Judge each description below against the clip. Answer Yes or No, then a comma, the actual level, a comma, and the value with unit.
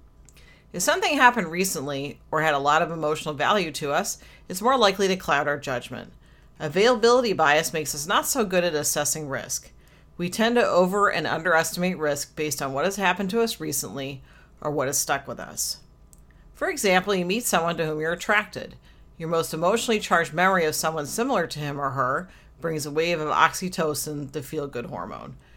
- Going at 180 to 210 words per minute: Yes, average, 190 wpm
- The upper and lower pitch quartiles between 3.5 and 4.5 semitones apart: Yes, average, 4.2 semitones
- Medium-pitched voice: Yes, medium, 160 Hz